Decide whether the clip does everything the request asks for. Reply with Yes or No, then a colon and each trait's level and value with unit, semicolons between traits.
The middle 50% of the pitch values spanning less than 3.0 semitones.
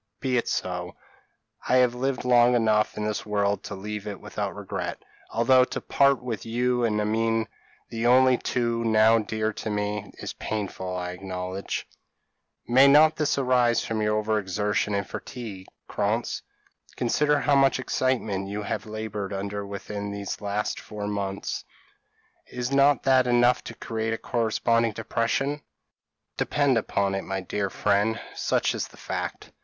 No: average, 3.3 semitones